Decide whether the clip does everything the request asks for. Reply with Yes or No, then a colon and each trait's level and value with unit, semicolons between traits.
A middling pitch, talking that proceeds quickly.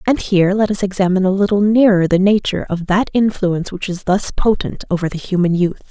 No: high, 195 Hz; fast, 215 wpm